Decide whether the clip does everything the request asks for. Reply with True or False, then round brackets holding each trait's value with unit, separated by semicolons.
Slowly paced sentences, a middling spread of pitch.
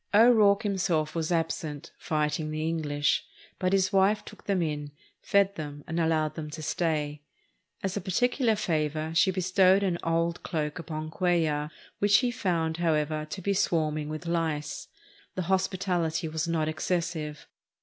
False (150 wpm; 3.4 semitones)